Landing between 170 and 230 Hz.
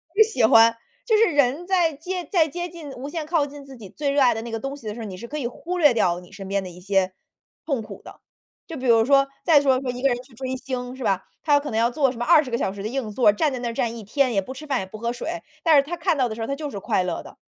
No: very high, 260 Hz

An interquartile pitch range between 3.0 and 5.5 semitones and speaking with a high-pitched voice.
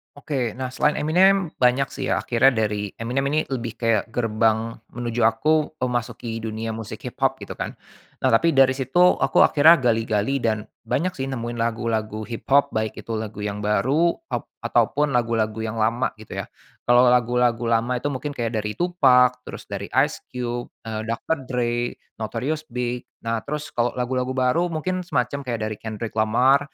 No: average, 3.3 semitones; low, 120 Hz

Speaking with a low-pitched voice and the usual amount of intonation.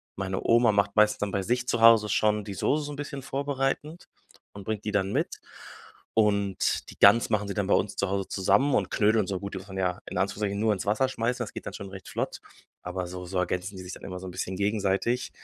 Yes: low, 105 Hz; average, 3.0 semitones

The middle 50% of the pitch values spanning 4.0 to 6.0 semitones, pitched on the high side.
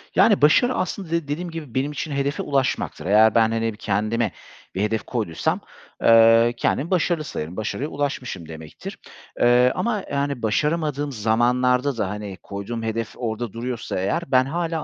No: average, 4.9 semitones; low, 125 Hz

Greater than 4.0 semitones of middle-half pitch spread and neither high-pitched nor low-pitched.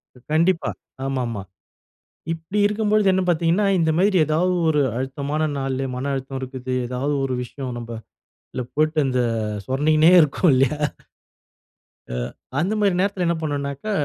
Yes: average, 4.8 semitones; medium, 150 Hz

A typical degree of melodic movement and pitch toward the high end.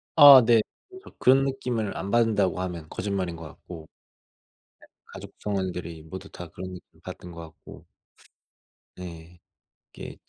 No: average, 5.0 semitones; very low, 95 Hz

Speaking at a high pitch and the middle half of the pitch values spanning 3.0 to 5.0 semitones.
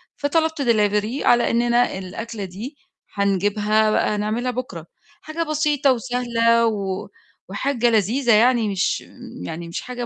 Yes: high, 230 Hz; average, 3.4 semitones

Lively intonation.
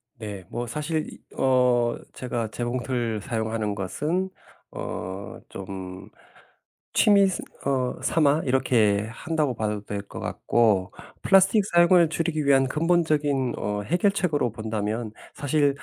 Yes: wide, 6.2 semitones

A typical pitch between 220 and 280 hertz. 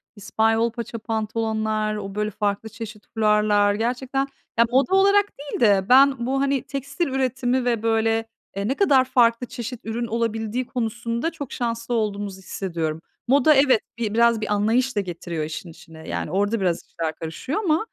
Yes: high, 225 Hz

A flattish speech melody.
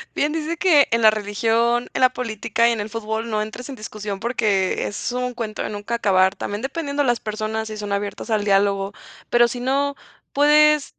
No: average, 3.3 semitones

